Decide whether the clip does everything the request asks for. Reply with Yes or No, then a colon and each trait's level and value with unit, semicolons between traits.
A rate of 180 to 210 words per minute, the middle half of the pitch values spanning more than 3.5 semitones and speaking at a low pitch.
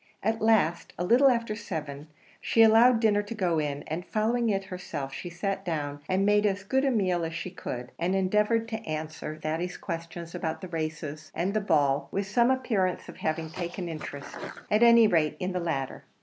No: average, 195 wpm; average, 5.0 semitones; medium, 185 Hz